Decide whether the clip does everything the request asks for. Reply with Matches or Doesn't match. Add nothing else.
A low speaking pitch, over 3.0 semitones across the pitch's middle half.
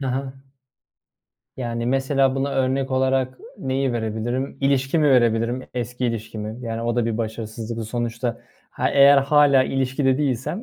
Doesn't match